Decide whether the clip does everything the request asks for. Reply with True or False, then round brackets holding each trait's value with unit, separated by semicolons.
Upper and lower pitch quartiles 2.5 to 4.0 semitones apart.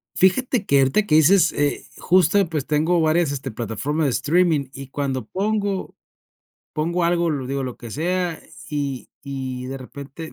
False (4.5 semitones)